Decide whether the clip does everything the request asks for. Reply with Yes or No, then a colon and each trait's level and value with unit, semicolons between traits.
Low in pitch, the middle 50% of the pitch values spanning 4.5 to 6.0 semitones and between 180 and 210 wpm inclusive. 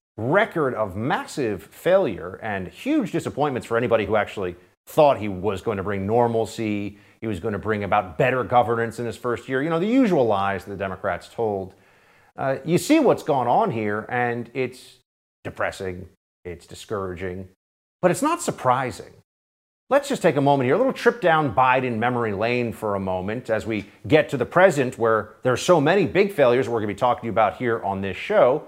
Yes: low, 115 Hz; average, 5.1 semitones; average, 200 wpm